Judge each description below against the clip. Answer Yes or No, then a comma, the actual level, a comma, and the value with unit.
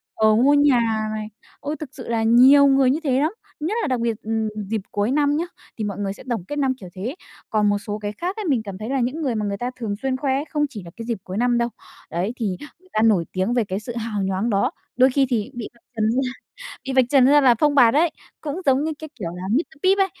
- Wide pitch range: No, average, 4.8 semitones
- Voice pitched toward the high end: Yes, high, 240 Hz